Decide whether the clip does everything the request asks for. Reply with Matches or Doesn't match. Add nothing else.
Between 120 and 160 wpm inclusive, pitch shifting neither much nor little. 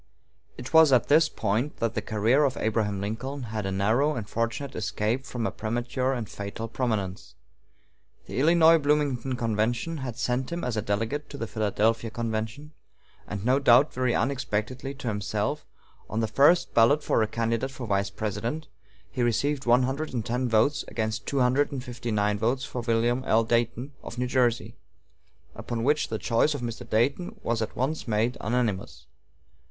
Doesn't match